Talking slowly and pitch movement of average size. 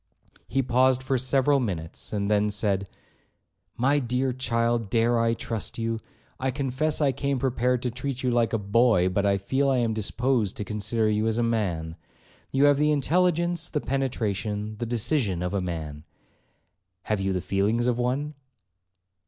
No: average, 170 wpm; average, 4.2 semitones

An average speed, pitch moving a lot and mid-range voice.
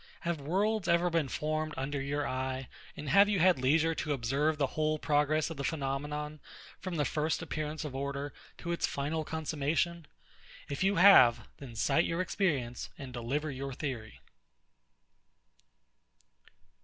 No: average, 150 wpm; average, 3.0 semitones; medium, 150 Hz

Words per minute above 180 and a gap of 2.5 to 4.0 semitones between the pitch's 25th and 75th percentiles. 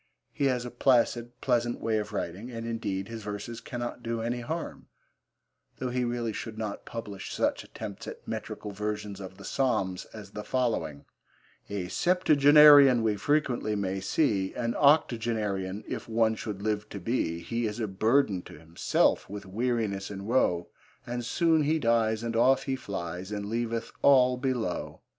No: average, 165 wpm; average, 3.4 semitones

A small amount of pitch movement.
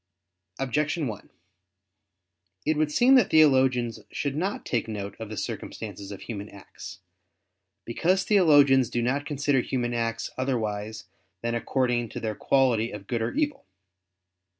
No: average, 4.6 semitones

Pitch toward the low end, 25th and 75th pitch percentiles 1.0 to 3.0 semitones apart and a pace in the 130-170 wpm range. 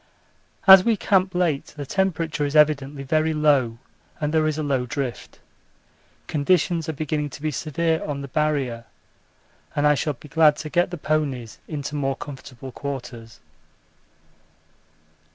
No: medium, 150 Hz; narrow, 2.4 semitones; average, 150 wpm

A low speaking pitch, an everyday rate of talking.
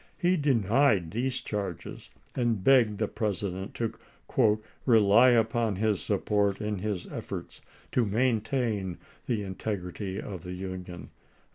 No: low, 105 Hz; slow, 125 wpm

